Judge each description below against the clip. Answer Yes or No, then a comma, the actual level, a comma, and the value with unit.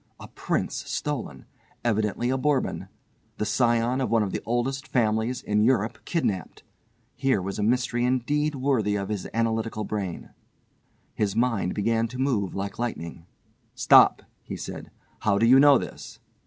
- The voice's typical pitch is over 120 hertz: No, low, 115 Hz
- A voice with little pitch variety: No, average, 3.5 semitones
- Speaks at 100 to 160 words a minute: Yes, average, 155 wpm